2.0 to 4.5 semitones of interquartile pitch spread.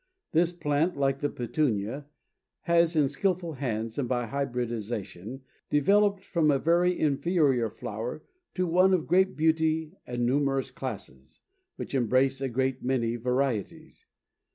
No: average, 4.9 semitones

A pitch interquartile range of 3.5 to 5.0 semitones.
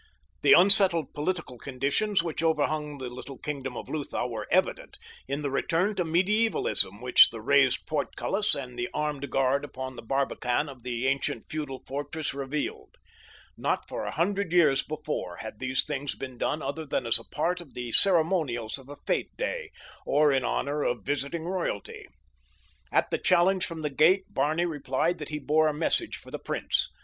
Yes: average, 4.0 semitones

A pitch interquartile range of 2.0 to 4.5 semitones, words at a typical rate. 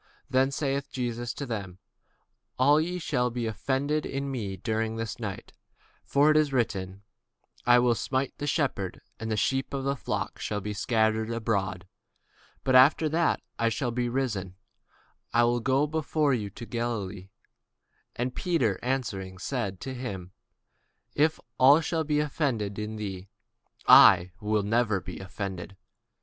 No: average, 4.9 semitones; average, 155 wpm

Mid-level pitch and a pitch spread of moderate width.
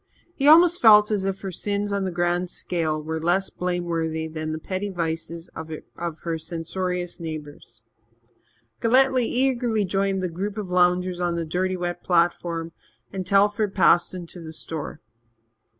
Yes: medium, 180 Hz; average, 3.2 semitones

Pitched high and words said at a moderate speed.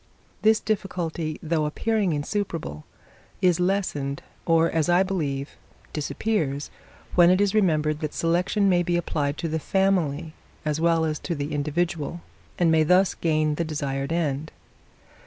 No: medium, 165 Hz; average, 145 wpm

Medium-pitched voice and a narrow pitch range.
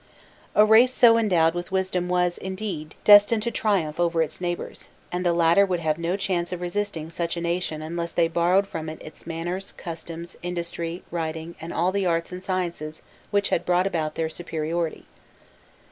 Yes: medium, 175 Hz; narrow, 2.2 semitones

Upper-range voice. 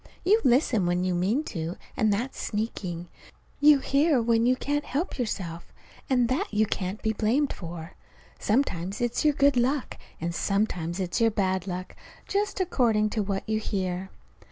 Yes: high, 215 Hz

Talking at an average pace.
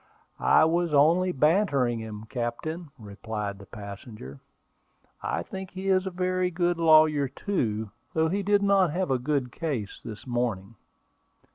Yes: average, 145 wpm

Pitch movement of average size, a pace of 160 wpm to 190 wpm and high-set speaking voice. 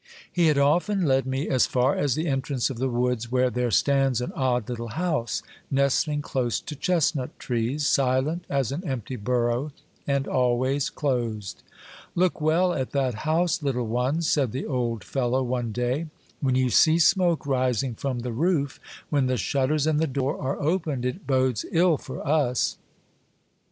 No: average, 3.4 semitones; average, 170 wpm; low, 135 Hz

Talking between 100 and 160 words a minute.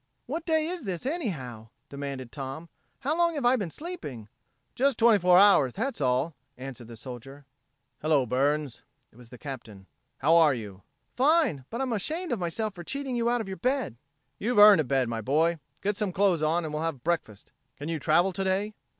No: average, 195 wpm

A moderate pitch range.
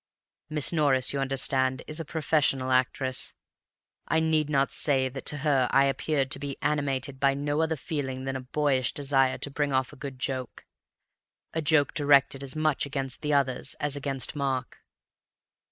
No: narrow, 2.0 semitones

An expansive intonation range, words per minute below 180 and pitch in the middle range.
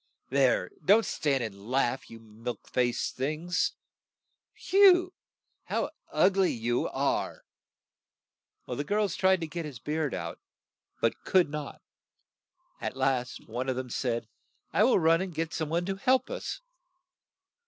Yes: wide, 7.1 semitones; average, 150 wpm; medium, 150 Hz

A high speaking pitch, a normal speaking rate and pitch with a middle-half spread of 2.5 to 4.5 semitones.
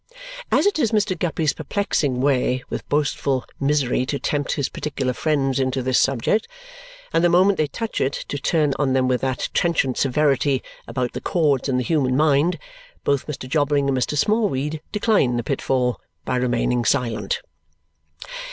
No: medium, 140 Hz; average, 165 wpm; average, 3.3 semitones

